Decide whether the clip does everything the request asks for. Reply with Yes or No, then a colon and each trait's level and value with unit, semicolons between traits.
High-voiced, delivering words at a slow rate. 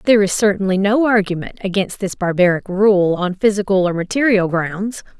No: high, 195 Hz; average, 160 wpm